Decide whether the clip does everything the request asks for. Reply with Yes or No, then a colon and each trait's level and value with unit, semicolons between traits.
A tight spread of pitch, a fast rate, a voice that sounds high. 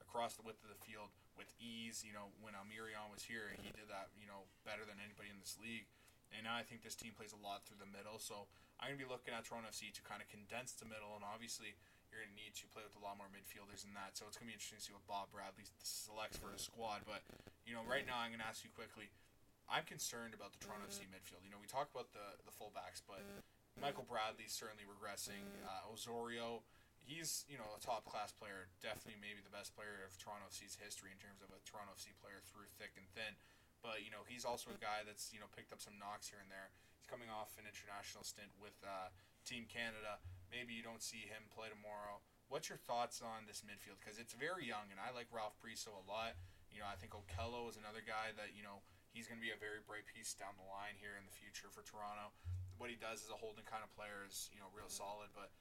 No: narrow, 1.9 semitones; fast, 255 wpm; low, 105 Hz